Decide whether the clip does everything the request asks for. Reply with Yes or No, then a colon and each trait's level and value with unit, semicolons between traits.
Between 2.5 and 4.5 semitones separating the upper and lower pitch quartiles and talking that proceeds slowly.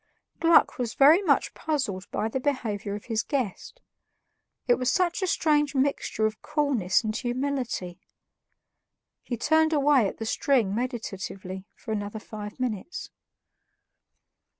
No: average, 5.3 semitones; slow, 130 wpm